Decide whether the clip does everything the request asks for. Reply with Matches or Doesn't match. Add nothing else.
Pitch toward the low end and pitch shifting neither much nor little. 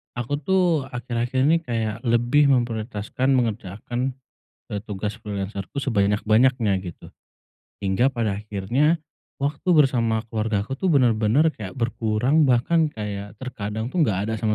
Matches